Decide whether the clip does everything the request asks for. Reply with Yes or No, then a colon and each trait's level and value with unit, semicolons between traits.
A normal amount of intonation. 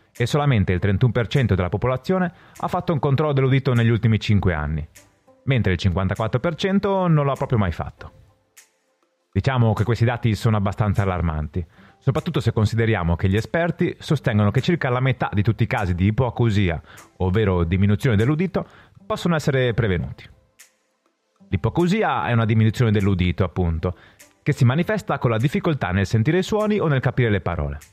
No: wide, 6.5 semitones